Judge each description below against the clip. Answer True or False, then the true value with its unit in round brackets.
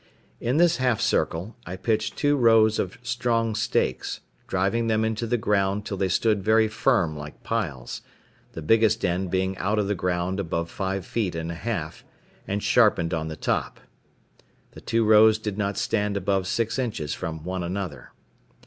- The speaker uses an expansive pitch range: False (3.7 semitones)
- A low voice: True (100 Hz)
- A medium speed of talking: True (175 wpm)